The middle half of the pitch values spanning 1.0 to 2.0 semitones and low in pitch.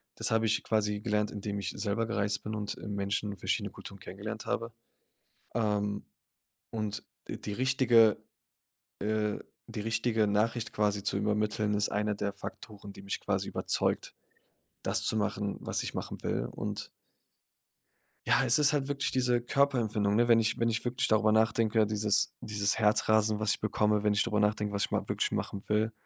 Yes: narrow, 1.6 semitones; low, 105 Hz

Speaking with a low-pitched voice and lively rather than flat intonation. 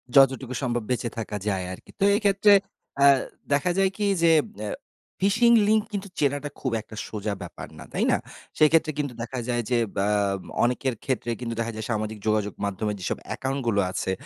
Yes: low, 125 Hz; wide, 6.0 semitones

